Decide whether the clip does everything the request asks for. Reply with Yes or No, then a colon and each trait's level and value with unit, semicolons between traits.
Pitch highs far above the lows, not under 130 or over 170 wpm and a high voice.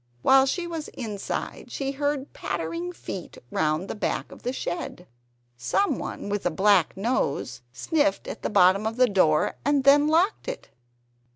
Yes: wide, 8.3 semitones; average, 160 wpm; high, 220 Hz